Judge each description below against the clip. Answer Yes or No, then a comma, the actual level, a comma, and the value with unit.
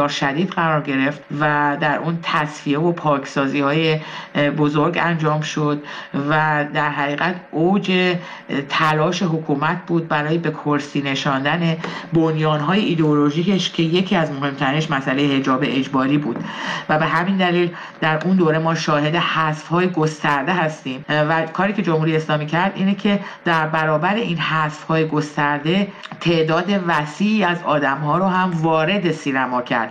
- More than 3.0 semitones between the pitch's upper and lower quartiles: No, narrow, 2.5 semitones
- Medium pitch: Yes, medium, 155 Hz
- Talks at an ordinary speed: Yes, average, 145 wpm